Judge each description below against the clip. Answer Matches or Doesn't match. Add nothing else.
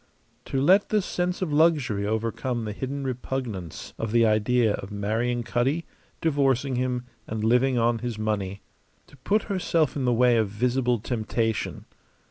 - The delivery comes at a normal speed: Matches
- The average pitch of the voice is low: Matches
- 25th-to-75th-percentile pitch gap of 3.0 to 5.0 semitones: Matches